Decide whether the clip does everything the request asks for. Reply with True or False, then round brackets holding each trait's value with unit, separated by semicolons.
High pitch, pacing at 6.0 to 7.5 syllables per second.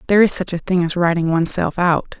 False (175 Hz; 6.5 syllables/s)